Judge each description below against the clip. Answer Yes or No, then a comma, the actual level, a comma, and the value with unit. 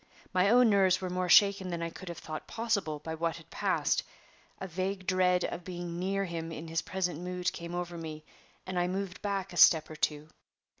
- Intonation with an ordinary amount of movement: No, narrow, 2.3 semitones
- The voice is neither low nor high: Yes, medium, 180 Hz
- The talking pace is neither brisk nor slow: No, fast, 210 wpm